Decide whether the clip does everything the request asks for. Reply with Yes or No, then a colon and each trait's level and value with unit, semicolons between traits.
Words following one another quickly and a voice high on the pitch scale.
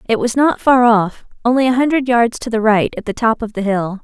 Yes: fast, 270 wpm; high, 230 Hz